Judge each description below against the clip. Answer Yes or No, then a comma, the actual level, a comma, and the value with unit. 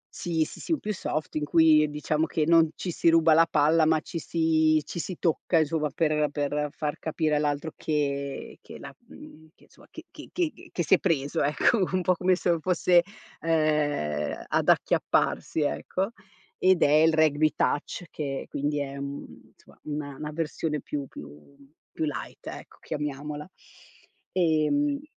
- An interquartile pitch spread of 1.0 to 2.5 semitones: Yes, narrow, 2.1 semitones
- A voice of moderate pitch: Yes, medium, 155 Hz